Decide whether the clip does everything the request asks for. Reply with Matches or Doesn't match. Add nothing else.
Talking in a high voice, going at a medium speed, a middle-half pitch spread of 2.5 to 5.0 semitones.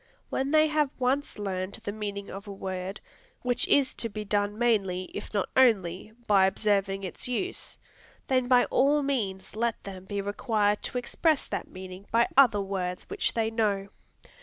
Matches